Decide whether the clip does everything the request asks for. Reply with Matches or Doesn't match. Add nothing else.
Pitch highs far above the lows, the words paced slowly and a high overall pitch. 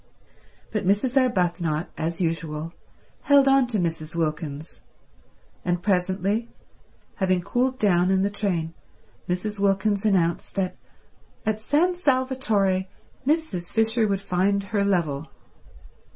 Doesn't match